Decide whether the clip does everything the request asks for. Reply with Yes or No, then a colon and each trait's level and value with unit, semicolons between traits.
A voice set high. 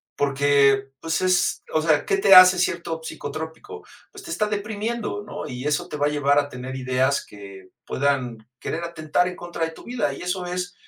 No: medium, 160 Hz